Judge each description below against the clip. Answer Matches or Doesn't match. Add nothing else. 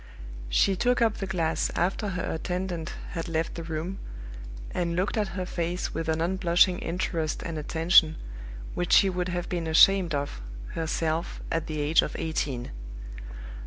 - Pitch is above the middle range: Doesn't match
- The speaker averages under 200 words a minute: Matches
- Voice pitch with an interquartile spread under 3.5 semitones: Matches